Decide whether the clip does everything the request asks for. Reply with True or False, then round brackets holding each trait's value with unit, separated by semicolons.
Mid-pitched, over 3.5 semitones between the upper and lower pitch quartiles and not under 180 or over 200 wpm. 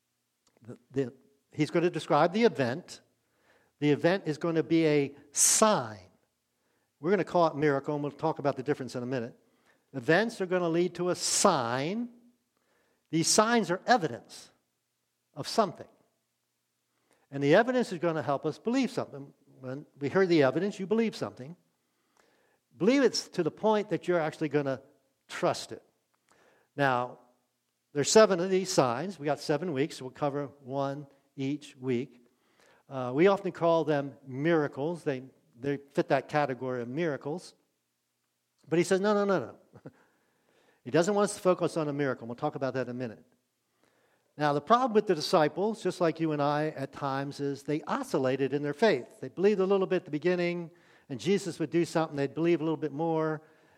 True (150 Hz; 4.4 semitones; 185 wpm)